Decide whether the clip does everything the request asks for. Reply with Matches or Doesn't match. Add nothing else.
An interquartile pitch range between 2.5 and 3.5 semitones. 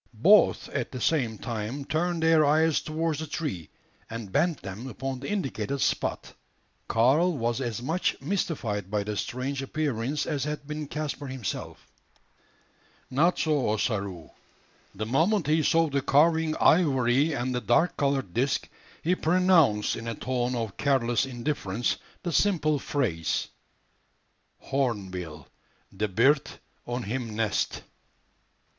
Doesn't match